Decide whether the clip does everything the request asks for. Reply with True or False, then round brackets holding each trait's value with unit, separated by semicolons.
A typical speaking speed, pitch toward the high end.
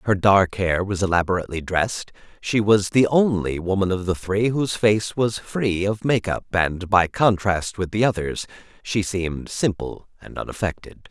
False (165 wpm; 100 Hz)